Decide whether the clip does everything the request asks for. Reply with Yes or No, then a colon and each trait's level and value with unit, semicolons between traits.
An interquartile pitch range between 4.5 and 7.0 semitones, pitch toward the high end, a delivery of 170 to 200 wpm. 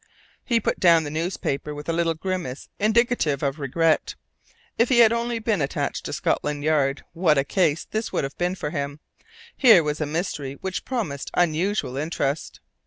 No: average, 5.1 semitones; medium, 165 Hz; average, 175 wpm